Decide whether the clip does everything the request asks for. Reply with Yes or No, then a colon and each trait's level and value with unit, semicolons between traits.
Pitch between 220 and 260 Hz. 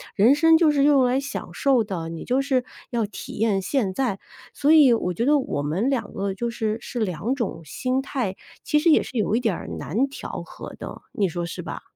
Yes: high, 235 Hz